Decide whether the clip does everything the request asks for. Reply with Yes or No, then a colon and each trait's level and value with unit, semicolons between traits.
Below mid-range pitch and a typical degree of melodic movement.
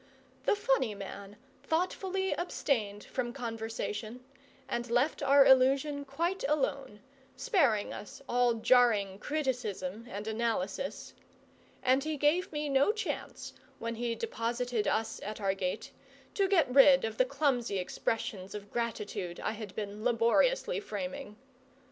No: high, 245 Hz; average, 4.8 semitones